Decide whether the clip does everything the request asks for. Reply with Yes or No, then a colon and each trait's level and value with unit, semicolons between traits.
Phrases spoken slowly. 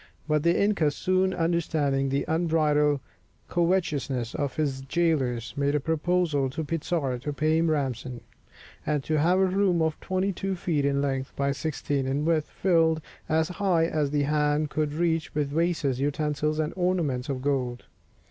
No: average, 165 wpm